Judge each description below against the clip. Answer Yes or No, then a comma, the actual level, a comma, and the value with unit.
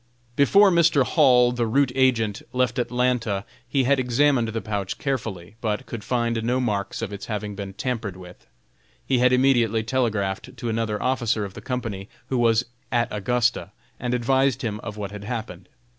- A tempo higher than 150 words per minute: Yes, average, 175 wpm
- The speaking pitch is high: No, low, 120 Hz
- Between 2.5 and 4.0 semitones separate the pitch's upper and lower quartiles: Yes, average, 3.3 semitones